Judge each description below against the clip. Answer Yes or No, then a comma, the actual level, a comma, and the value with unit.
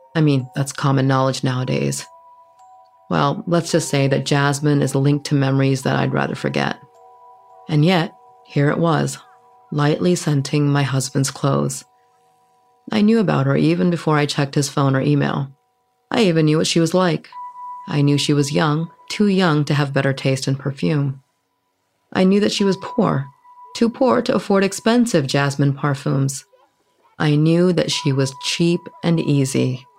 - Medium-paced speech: Yes, average, 165 wpm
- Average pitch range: No, wide, 8.0 semitones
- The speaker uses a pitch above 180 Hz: No, medium, 155 Hz